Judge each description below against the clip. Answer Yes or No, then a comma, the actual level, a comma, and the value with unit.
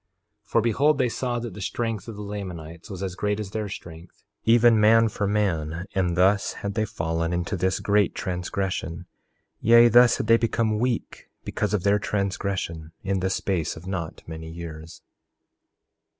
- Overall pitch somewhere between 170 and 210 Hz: No, low, 100 Hz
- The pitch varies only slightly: No, average, 4.0 semitones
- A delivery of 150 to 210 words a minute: Yes, average, 175 wpm